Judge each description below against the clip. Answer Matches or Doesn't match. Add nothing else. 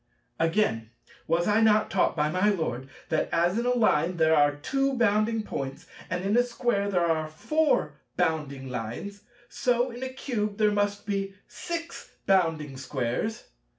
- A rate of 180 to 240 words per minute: Doesn't match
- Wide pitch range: Matches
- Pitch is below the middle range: Doesn't match